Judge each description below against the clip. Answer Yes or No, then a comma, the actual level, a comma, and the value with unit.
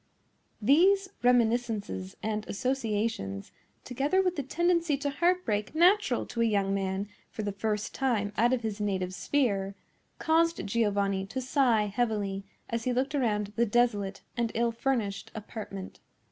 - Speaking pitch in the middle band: No, high, 230 Hz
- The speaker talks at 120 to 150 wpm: Yes, average, 145 wpm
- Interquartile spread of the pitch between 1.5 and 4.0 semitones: No, average, 4.8 semitones